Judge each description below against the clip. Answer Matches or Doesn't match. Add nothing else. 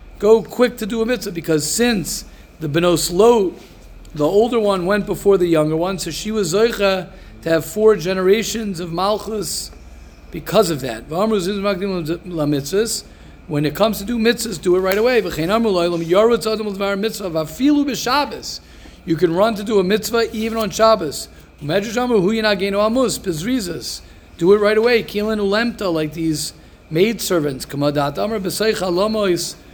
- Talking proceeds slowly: Matches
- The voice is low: Doesn't match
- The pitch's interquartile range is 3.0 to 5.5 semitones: Matches